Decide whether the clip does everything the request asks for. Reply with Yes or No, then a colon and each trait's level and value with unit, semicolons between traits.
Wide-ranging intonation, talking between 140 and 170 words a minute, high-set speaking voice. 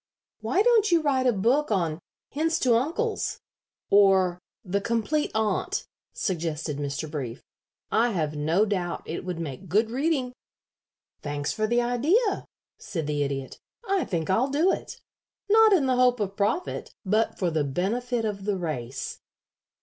Yes: wide, 7.8 semitones; average, 155 wpm; high, 210 Hz